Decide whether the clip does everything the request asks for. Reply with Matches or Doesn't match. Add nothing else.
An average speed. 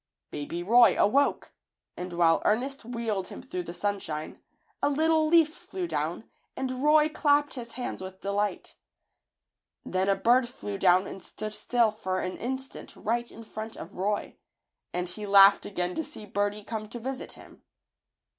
Matches